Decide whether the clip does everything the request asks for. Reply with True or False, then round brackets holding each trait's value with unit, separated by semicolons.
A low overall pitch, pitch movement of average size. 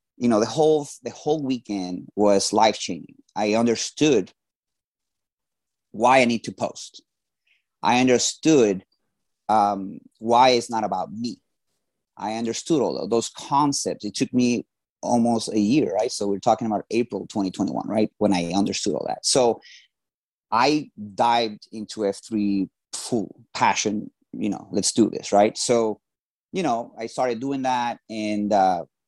True (110 Hz; 3.1 semitones)